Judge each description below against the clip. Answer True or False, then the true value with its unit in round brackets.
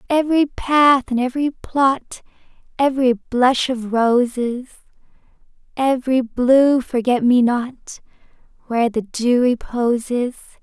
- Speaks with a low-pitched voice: False (255 Hz)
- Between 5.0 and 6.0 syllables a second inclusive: False (3.9 syllables/s)